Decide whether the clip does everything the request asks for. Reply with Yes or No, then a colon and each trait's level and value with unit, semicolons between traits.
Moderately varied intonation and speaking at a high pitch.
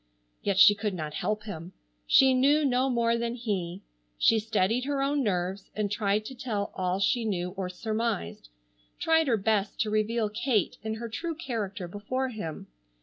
Yes: average, 3.8 semitones; high, 215 Hz